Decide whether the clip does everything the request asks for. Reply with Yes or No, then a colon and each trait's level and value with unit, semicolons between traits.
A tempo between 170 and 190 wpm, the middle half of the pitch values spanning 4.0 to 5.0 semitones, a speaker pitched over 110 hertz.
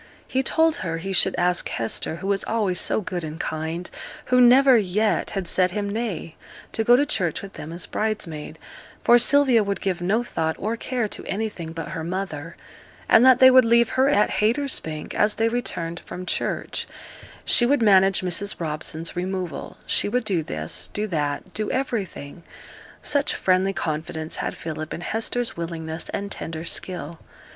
No: average, 175 wpm; wide, 5.4 semitones; high, 190 Hz